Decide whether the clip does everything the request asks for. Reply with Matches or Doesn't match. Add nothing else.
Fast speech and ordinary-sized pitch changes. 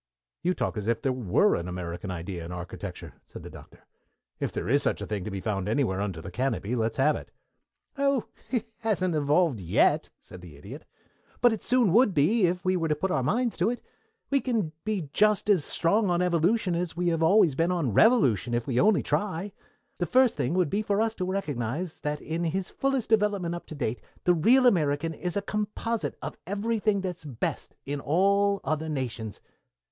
Doesn't match